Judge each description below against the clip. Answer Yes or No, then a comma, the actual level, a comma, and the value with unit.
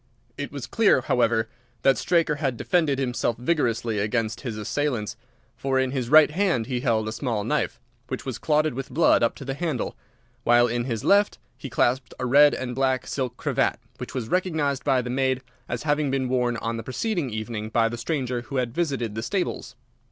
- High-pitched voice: No, low, 130 Hz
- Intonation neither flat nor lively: Yes, average, 3.5 semitones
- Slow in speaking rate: No, average, 195 wpm